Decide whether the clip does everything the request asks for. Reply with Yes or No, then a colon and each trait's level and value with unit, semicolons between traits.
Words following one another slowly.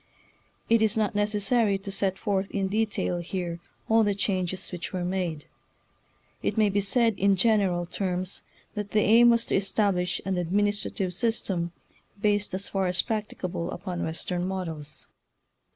No: average, 155 wpm